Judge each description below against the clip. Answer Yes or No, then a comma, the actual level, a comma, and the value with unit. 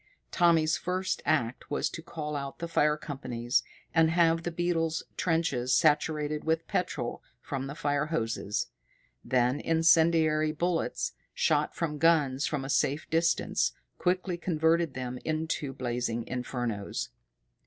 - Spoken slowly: Yes, slow, 130 wpm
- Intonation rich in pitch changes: No, average, 3.7 semitones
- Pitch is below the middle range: No, medium, 155 Hz